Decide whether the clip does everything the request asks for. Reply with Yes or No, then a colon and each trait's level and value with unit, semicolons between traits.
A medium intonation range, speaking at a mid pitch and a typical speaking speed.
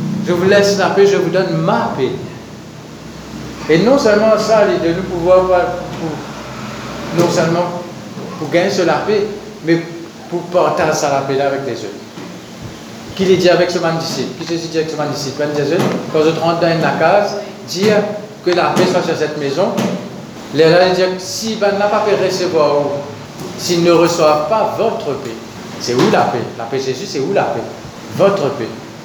Yes: average, 3.8 semitones; medium, 175 Hz; average, 190 wpm